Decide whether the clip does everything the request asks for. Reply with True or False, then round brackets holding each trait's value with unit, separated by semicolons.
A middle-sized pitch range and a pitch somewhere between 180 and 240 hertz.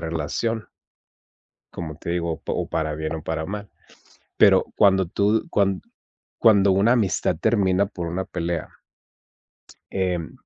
False (3.5 semitones; 95 Hz)